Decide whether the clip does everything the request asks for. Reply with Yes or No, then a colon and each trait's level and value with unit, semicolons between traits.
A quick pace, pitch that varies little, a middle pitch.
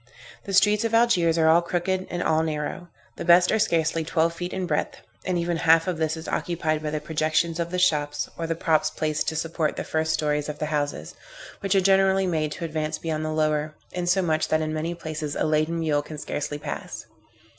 Yes: fast, 215 wpm; narrow, 2.1 semitones; medium, 160 Hz